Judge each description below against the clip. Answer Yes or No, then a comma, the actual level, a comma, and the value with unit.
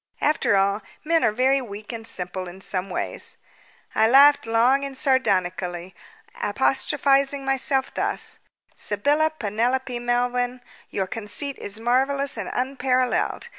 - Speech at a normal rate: No, slow, 125 wpm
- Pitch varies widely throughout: No, average, 4.8 semitones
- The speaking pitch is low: No, high, 245 Hz